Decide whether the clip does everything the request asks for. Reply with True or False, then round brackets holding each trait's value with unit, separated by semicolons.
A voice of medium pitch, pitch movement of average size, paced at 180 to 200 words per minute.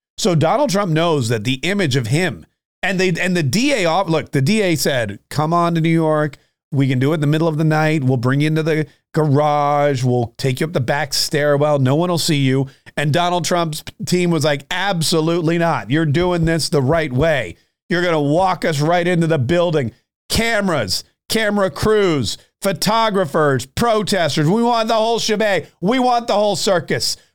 True (160 Hz; 3.9 semitones; 195 wpm)